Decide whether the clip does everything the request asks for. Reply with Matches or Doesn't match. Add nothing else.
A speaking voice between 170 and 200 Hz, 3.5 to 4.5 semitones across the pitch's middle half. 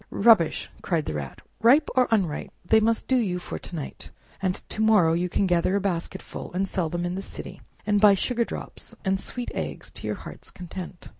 Matches